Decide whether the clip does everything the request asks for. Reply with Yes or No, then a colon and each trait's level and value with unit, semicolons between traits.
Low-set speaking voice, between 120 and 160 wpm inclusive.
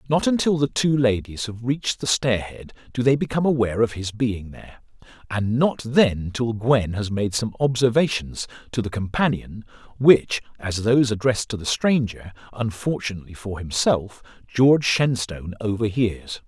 Yes: low, 115 Hz; average, 155 wpm